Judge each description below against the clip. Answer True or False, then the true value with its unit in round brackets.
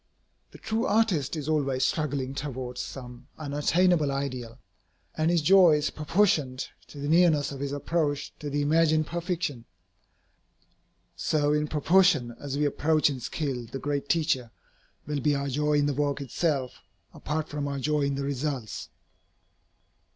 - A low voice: False (145 Hz)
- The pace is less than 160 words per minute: True (150 wpm)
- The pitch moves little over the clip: True (2.3 semitones)